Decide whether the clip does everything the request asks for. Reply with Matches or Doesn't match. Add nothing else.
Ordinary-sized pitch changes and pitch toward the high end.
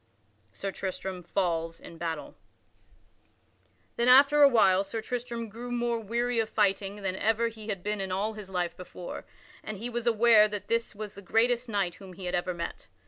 Matches